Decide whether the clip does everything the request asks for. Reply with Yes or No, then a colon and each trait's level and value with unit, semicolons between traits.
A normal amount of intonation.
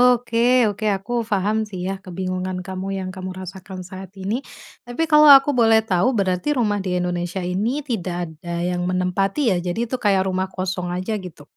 Yes: average, 3.6 semitones